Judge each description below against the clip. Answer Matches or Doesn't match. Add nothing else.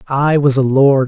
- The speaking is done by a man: Matches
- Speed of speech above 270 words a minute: Doesn't match